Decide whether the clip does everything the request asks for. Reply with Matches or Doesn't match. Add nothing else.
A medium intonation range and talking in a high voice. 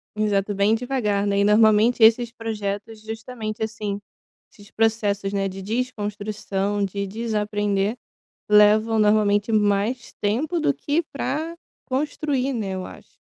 Doesn't match